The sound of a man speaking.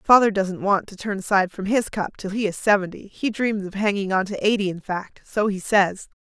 No: female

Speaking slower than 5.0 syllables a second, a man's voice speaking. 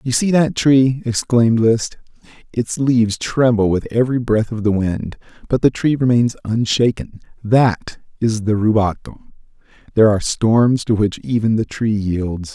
Yes: 4.5 syllables/s; male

